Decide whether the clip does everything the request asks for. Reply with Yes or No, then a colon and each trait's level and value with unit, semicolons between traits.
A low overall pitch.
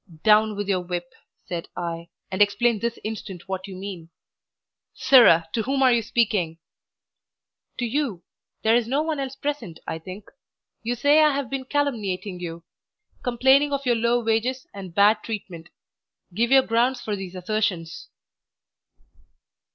No: high, 220 Hz